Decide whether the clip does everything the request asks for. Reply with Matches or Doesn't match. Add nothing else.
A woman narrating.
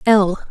Matches